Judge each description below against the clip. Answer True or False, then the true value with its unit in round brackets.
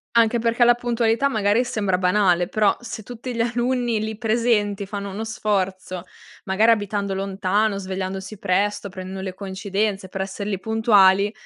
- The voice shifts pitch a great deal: False (2.7 semitones)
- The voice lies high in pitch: True (205 Hz)